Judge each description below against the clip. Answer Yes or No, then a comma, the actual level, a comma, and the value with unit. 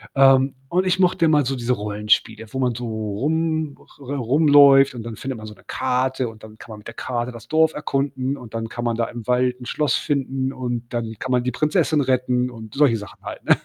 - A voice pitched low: Yes, low, 125 Hz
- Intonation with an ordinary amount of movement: Yes, average, 3.2 semitones